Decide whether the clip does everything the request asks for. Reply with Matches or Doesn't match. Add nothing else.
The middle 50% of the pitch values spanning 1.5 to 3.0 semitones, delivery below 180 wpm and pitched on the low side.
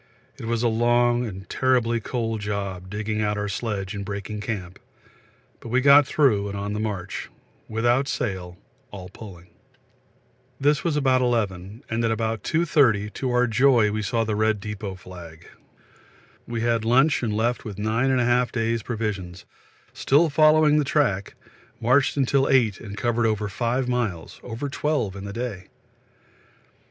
Doesn't match